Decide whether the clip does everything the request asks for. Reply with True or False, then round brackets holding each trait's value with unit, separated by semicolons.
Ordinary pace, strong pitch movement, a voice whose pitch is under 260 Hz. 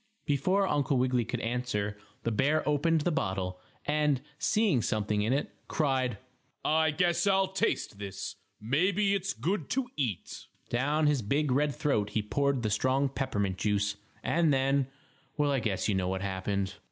True (165 wpm; 6.3 semitones; 135 Hz)